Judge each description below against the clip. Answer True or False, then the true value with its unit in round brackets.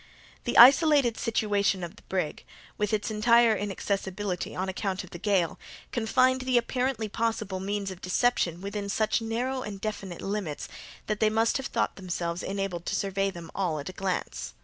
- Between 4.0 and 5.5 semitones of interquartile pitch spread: False (3.3 semitones)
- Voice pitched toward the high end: True (205 Hz)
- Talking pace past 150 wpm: True (170 wpm)